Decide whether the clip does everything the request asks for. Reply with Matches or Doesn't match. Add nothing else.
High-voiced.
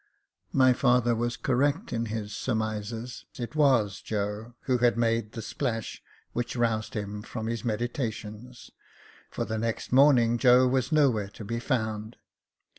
Doesn't match